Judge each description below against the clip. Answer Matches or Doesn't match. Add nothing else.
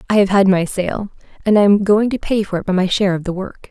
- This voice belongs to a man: Doesn't match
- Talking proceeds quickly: Matches